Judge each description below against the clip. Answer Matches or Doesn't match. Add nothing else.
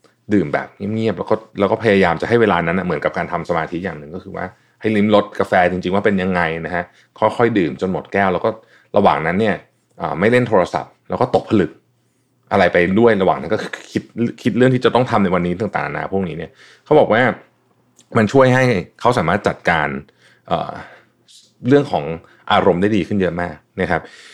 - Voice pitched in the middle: Doesn't match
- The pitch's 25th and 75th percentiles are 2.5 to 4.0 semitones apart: Doesn't match